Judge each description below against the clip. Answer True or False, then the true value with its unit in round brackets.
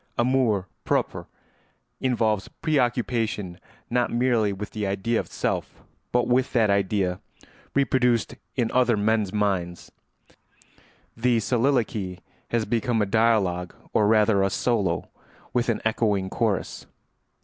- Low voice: True (110 Hz)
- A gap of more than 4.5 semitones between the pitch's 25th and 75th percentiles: False (3.3 semitones)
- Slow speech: True (115 wpm)